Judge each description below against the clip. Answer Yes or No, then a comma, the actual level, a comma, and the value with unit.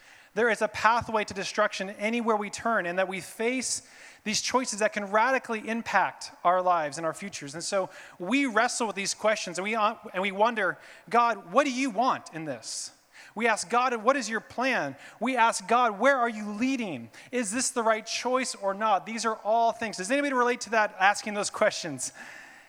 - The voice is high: Yes, high, 220 Hz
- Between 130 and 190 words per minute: No, average, 200 wpm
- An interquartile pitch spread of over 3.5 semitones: No, average, 3.0 semitones